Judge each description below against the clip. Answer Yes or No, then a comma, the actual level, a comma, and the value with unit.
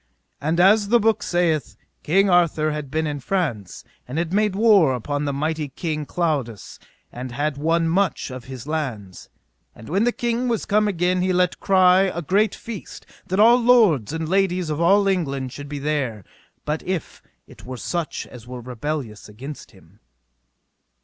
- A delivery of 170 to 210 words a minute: Yes, average, 175 wpm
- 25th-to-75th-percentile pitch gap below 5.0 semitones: No, wide, 5.6 semitones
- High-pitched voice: No, medium, 160 Hz